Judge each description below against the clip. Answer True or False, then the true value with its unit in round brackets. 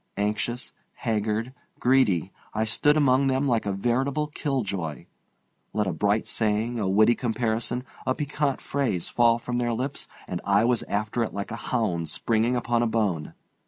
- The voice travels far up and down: False (3.3 semitones)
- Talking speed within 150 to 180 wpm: True (160 wpm)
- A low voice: True (115 Hz)